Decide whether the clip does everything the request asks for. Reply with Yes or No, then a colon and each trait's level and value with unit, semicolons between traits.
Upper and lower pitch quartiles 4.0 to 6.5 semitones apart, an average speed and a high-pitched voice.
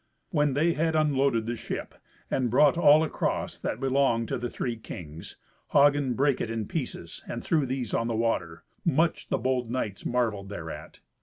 No: average, 4.3 semitones; average, 175 wpm; low, 125 Hz